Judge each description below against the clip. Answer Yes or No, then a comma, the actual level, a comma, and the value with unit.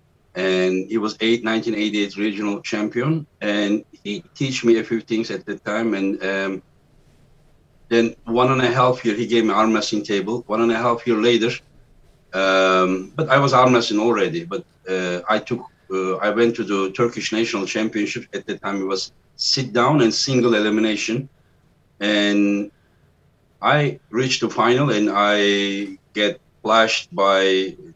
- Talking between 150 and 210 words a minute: Yes, average, 165 wpm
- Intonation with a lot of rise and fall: No, average, 2.8 semitones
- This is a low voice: Yes, low, 110 Hz